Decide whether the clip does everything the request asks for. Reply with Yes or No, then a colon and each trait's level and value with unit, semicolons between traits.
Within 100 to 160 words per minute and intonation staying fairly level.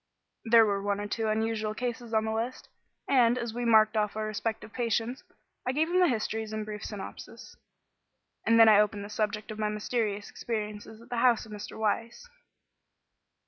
No: average, 185 wpm; narrow, 1.7 semitones